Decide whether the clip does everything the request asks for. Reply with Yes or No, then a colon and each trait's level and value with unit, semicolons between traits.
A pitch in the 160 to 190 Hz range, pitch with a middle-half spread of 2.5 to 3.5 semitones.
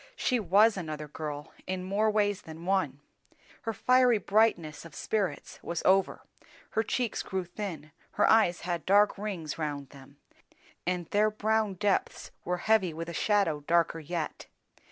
No: medium, 185 Hz; average, 4.4 semitones